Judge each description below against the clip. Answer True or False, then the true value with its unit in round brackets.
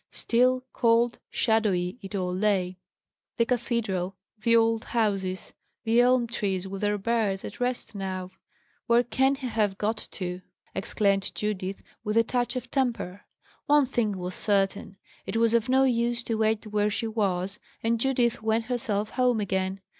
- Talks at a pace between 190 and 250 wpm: False (160 wpm)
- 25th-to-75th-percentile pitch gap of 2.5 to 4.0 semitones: True (3.4 semitones)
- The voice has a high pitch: True (220 Hz)